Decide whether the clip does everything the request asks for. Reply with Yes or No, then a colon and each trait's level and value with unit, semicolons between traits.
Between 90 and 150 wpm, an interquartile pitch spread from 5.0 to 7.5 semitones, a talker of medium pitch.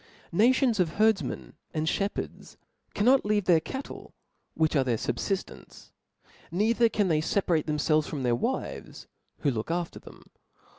Yes: average, 140 wpm; wide, 5.5 semitones; medium, 175 Hz